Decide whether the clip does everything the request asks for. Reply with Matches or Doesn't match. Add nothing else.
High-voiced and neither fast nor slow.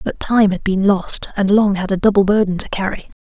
Doesn't match